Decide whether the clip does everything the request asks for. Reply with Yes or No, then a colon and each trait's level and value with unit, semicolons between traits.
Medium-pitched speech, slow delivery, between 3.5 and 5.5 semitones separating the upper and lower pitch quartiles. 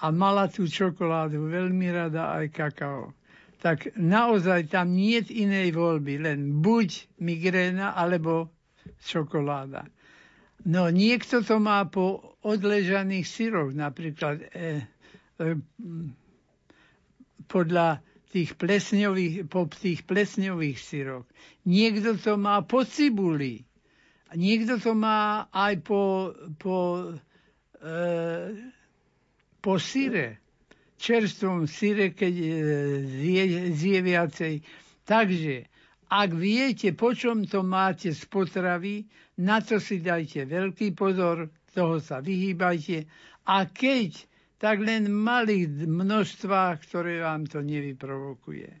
Yes: medium, 180 Hz; slow, 105 wpm; average, 4.0 semitones